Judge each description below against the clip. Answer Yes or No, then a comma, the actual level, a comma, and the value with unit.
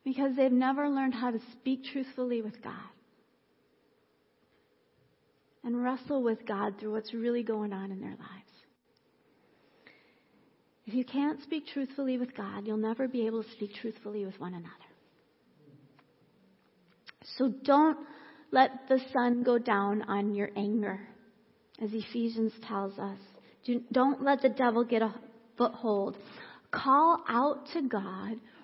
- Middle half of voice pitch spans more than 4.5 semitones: No, average, 3.5 semitones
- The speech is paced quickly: No, slow, 135 wpm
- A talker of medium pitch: No, high, 240 Hz